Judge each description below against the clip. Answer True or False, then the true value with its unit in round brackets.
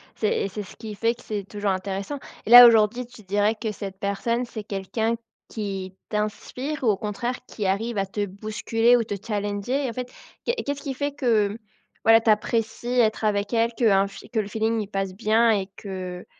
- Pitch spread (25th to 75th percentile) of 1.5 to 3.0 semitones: True (2.7 semitones)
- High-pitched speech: True (215 Hz)